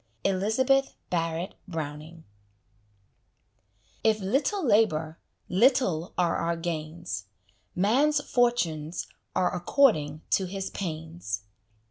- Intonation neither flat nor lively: No, wide, 5.7 semitones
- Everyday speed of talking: No, slow, 85 wpm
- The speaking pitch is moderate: Yes, medium, 180 Hz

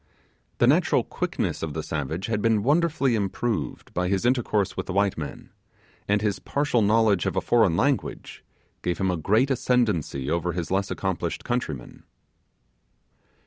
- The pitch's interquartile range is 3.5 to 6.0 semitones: Yes, wide, 5.4 semitones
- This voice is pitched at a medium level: No, low, 100 Hz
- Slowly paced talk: No, average, 155 wpm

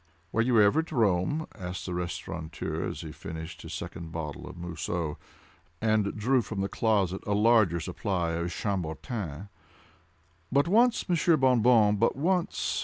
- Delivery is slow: No, average, 155 wpm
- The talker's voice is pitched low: Yes, low, 100 Hz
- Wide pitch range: Yes, wide, 5.8 semitones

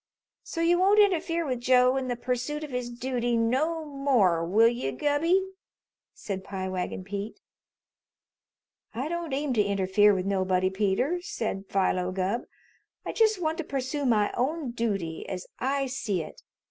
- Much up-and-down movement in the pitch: Yes, wide, 7.1 semitones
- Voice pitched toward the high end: Yes, high, 245 Hz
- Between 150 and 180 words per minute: Yes, average, 160 wpm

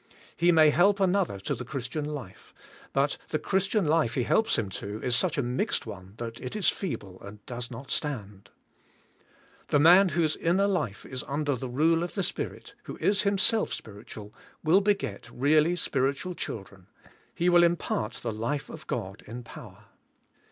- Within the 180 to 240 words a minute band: Yes, average, 195 wpm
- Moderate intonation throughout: No, wide, 7.2 semitones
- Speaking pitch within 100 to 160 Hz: Yes, medium, 140 Hz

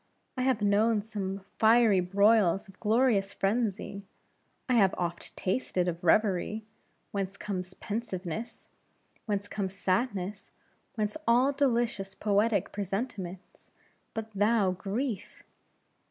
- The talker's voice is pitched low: No, high, 205 Hz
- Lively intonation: No, average, 2.8 semitones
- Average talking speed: No, slow, 110 wpm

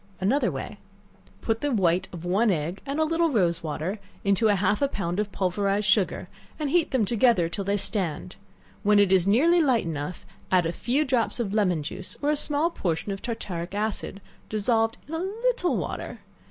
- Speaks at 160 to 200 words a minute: Yes, average, 190 wpm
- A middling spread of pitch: No, wide, 6.2 semitones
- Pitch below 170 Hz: No, high, 205 Hz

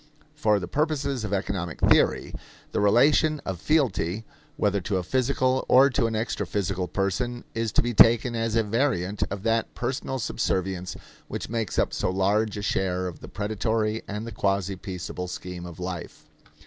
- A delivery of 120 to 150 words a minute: No, average, 170 wpm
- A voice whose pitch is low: Yes, low, 105 Hz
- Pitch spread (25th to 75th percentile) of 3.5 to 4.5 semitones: Yes, average, 3.9 semitones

